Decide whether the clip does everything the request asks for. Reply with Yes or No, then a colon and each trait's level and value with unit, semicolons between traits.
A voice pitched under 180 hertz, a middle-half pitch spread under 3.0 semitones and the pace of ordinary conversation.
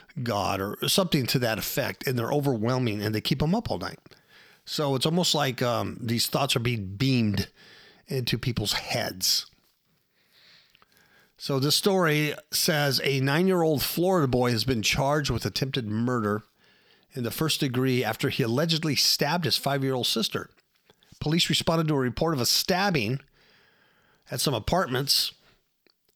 No: low, 135 Hz; average, 4.2 semitones; average, 160 wpm